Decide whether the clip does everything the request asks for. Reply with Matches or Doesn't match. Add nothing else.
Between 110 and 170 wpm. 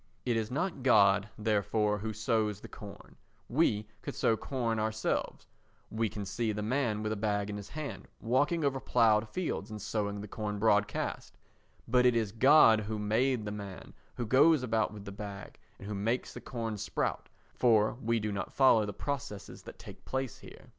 Doesn't match